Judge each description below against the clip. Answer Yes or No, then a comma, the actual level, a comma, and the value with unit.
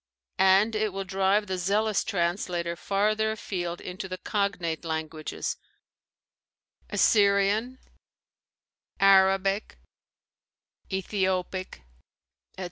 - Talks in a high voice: Yes, high, 195 Hz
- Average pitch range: No, narrow, 2.2 semitones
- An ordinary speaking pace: No, slow, 80 wpm